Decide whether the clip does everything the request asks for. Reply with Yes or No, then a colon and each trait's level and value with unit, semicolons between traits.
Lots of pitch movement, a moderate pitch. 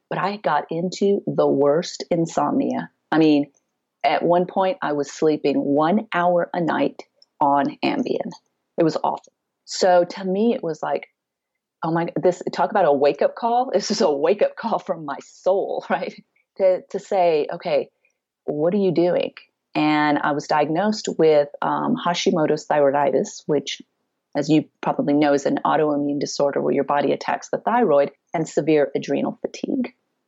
No: average, 4.3 semitones; medium, 165 Hz